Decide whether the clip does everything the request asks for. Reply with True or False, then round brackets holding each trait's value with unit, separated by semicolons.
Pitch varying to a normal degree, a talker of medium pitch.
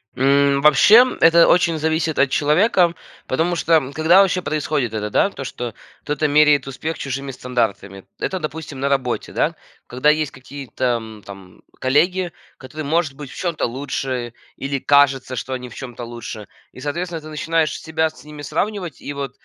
True (3.7 semitones; 145 Hz)